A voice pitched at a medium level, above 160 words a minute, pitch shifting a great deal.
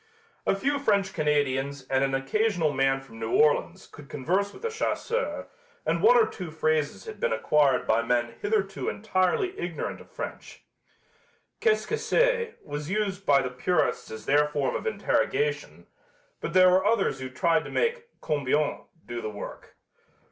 Yes: medium, 160 Hz; average, 170 wpm; wide, 8.0 semitones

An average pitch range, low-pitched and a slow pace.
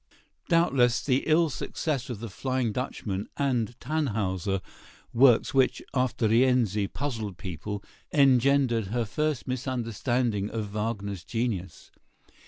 Yes: average, 3.9 semitones; low, 120 Hz; slow, 115 wpm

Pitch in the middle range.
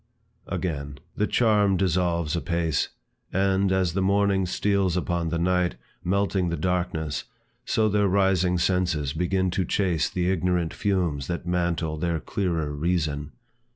No: very low, 90 Hz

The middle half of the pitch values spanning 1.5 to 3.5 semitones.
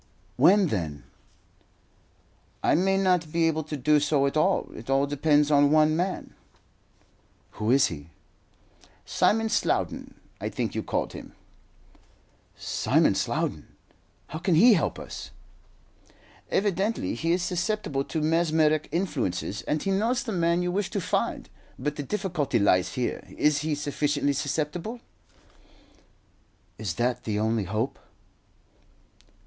No: average, 4.7 semitones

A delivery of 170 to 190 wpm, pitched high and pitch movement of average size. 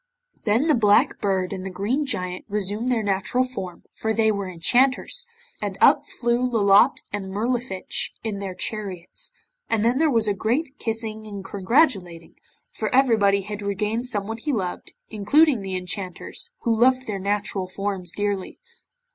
No: average, 155 wpm; high, 210 Hz; average, 3.6 semitones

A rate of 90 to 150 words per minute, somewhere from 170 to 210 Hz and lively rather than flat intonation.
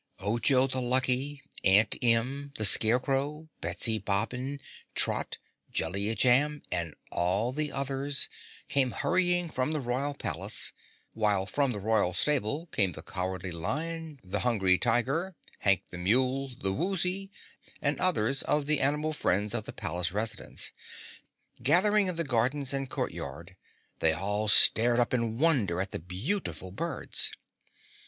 No: average, 140 wpm; low, 125 Hz; wide, 6.0 semitones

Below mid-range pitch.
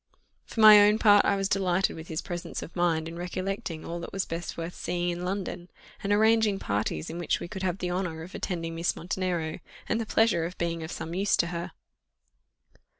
No: medium, 175 Hz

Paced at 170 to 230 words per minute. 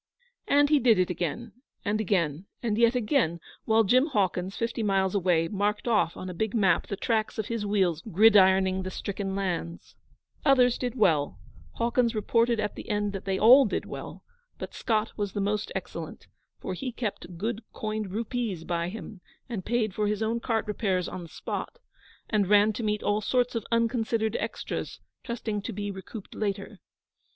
Yes: average, 180 wpm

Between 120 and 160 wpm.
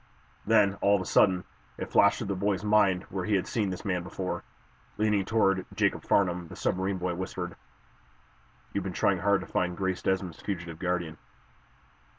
No: average, 175 wpm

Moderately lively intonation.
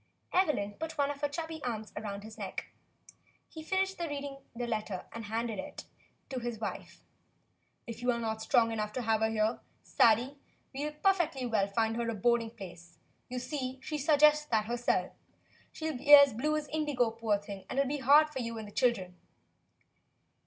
Yes: average, 4.8 semitones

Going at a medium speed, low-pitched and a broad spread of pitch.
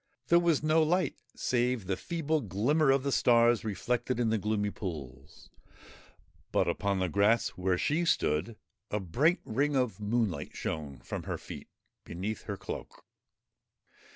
Yes: average, 150 wpm; low, 115 Hz; wide, 6.7 semitones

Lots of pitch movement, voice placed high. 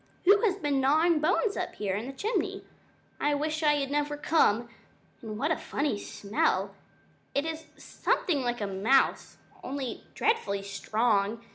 Yes: wide, 6.4 semitones; very high, 280 Hz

